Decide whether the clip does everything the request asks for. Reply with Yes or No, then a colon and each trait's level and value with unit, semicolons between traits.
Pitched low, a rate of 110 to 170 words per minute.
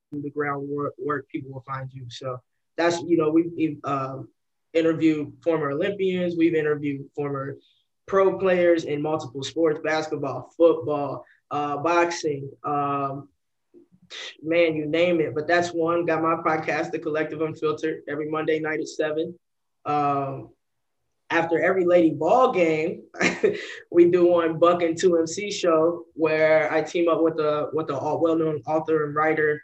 No: medium, 155 Hz; average, 150 wpm